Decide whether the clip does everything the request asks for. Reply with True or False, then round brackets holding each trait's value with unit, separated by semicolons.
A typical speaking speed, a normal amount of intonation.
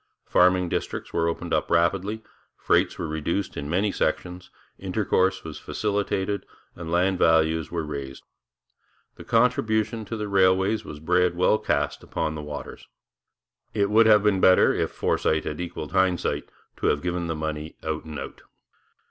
True (155 wpm; 4.0 semitones)